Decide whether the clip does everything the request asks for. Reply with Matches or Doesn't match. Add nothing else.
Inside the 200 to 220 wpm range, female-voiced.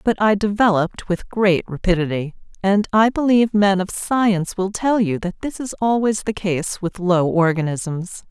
Doesn't match